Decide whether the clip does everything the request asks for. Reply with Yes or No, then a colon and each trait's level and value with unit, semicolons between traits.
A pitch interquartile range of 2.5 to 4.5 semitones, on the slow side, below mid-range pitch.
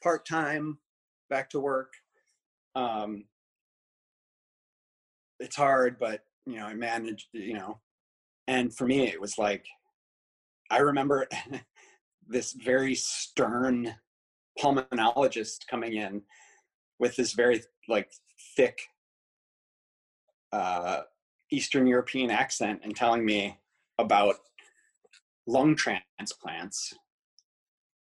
No: average, 5.3 semitones; slow, 90 wpm; low, 125 Hz